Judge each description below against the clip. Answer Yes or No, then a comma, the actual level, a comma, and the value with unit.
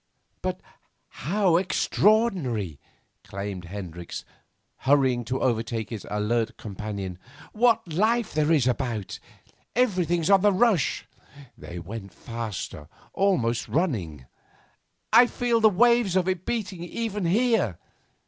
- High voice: No, medium, 150 Hz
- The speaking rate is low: Yes, slow, 110 wpm